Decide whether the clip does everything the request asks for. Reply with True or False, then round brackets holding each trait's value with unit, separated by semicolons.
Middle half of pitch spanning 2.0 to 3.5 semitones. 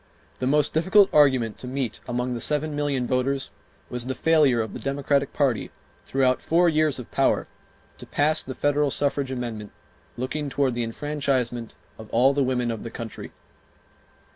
True (3.0 semitones)